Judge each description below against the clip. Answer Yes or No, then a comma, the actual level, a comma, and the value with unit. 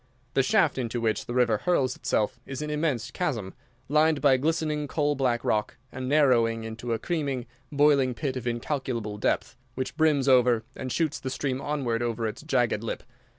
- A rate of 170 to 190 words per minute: Yes, average, 180 wpm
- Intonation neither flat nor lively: Yes, average, 4.0 semitones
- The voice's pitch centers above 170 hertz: No, low, 130 Hz